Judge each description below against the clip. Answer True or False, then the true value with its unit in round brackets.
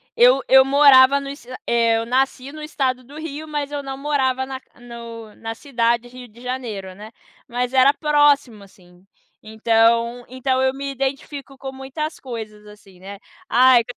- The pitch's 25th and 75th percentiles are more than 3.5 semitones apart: False (3.1 semitones)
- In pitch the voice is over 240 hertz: True (255 Hz)